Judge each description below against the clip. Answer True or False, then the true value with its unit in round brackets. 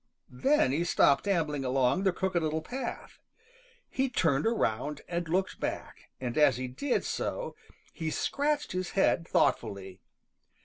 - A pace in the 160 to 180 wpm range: False (140 wpm)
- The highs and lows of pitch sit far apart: True (6.4 semitones)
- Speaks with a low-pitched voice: False (165 Hz)